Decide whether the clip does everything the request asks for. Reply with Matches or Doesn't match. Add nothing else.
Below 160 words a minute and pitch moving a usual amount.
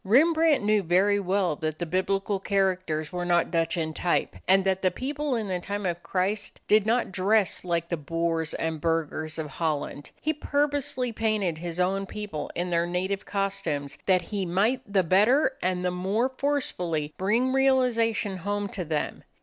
Doesn't match